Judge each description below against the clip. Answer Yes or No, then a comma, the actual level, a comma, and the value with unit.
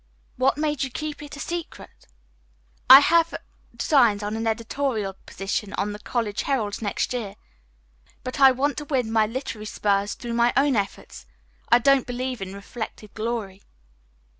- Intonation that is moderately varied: Yes, average, 4.6 semitones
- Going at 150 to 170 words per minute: Yes, average, 160 wpm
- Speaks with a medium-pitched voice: No, high, 235 Hz